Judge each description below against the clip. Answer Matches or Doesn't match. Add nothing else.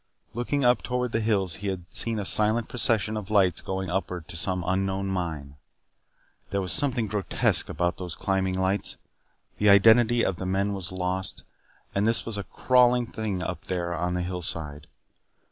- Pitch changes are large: Doesn't match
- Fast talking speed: Doesn't match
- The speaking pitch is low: Matches